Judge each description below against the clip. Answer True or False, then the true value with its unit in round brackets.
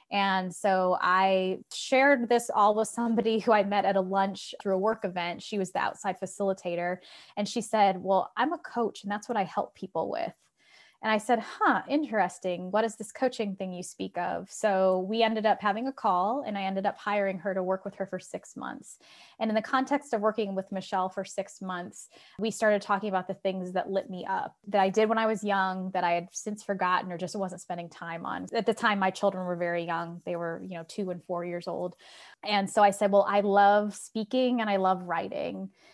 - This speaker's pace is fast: True (230 wpm)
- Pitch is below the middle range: False (195 Hz)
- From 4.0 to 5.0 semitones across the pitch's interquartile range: False (2.7 semitones)